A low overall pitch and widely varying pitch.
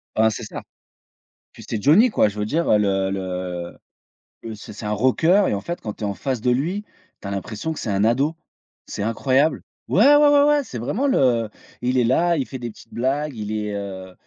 Yes: low, 115 Hz; wide, 6.8 semitones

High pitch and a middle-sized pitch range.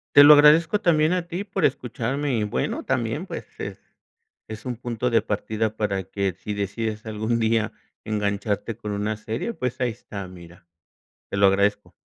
No: low, 110 Hz; average, 3.8 semitones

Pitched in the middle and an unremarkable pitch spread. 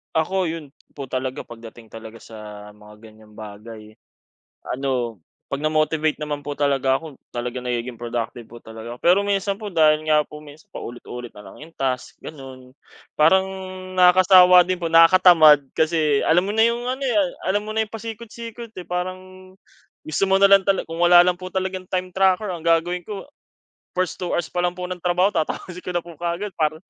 No: medium, 165 Hz; wide, 5.8 semitones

